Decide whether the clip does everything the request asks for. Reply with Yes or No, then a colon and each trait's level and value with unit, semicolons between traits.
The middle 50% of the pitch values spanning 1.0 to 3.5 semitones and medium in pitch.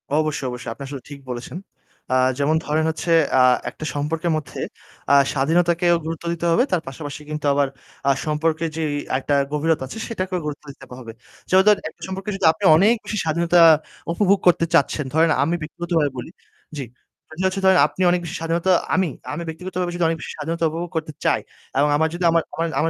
Yes: average, 2.7 semitones; medium, 165 Hz